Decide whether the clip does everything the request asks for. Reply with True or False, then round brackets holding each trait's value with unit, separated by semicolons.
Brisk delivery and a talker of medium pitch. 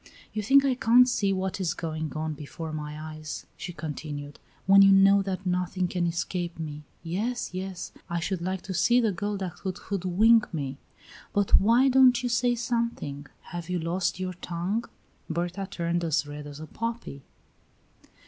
False (175 wpm; 180 Hz)